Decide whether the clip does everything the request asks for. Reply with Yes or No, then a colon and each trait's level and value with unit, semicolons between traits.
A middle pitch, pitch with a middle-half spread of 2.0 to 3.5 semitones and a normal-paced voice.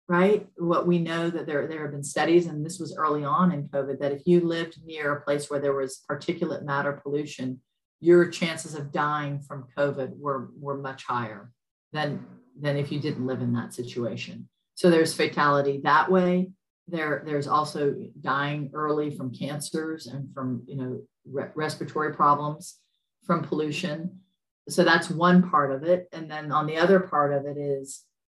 Yes: medium, 150 Hz; average, 3.0 semitones; average, 180 wpm